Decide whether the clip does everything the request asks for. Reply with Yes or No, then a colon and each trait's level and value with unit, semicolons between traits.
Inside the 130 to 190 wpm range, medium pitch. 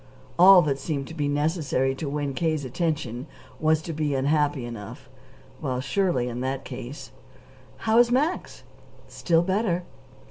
Yes: average, 145 wpm; medium, 150 Hz